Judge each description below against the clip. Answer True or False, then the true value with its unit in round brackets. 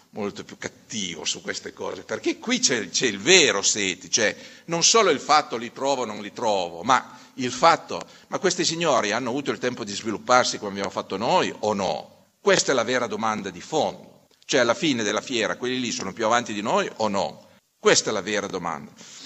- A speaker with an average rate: False (210 wpm)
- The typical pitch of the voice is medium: True (150 Hz)